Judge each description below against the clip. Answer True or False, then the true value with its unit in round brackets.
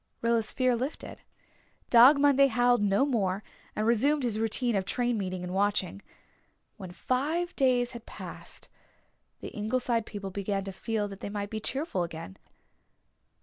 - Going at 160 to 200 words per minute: False (150 wpm)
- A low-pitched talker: False (225 Hz)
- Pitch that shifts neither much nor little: True (4.1 semitones)